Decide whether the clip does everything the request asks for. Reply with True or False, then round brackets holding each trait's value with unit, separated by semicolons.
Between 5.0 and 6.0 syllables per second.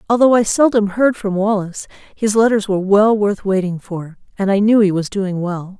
True (5.3 syllables/s)